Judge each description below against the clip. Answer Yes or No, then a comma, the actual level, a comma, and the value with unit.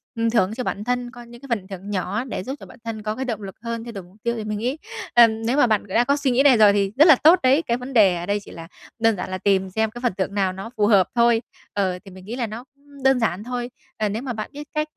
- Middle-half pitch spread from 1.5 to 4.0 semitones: Yes, average, 3.6 semitones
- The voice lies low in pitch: No, high, 225 Hz